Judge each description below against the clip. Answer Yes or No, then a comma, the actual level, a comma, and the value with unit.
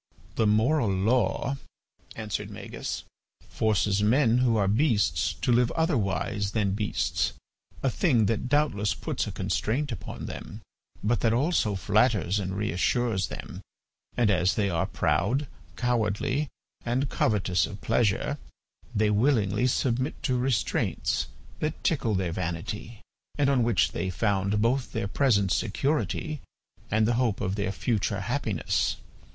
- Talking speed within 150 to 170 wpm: No, slow, 135 wpm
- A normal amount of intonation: Yes, average, 4.0 semitones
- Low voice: Yes, low, 110 Hz